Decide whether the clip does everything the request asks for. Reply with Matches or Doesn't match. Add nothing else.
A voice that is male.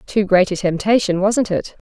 Doesn't match